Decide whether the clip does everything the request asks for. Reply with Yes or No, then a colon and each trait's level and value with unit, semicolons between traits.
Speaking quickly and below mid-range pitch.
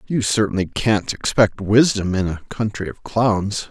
No: average, 160 wpm; low, 105 Hz